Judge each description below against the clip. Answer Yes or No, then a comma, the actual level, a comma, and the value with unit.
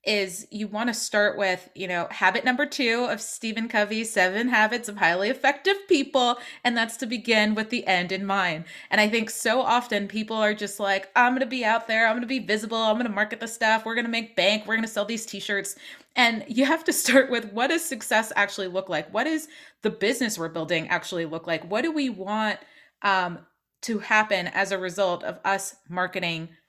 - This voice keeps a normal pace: No, fast, 210 wpm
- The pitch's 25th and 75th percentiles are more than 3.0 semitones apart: Yes, average, 3.5 semitones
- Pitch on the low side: No, high, 215 Hz